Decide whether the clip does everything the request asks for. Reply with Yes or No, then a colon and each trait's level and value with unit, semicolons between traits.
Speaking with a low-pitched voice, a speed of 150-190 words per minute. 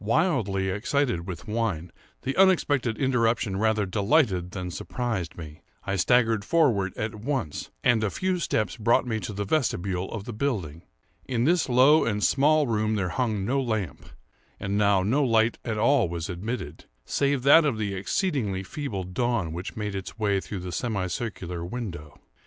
Yes: low, 110 Hz; average, 170 wpm